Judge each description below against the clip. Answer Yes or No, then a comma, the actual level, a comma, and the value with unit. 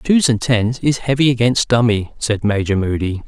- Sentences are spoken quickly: No, average, 185 wpm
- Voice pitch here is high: No, low, 115 Hz